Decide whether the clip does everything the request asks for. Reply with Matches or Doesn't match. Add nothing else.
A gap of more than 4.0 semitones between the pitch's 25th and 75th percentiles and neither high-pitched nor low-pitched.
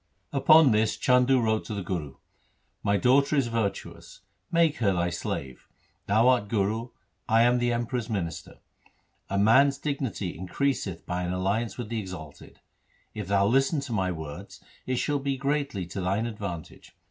Doesn't match